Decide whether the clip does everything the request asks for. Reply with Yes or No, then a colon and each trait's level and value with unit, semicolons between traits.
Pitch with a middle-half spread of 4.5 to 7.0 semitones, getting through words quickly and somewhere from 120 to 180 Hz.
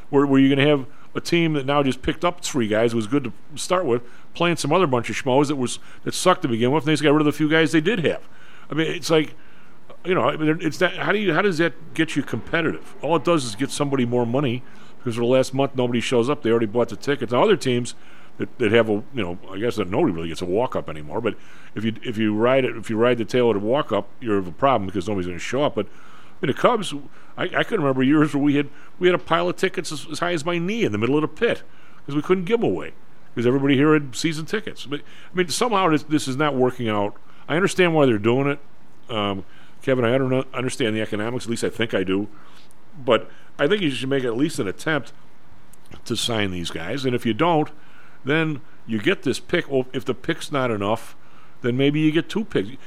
Yes: average, 4.9 semitones; fast, 265 wpm; medium, 140 Hz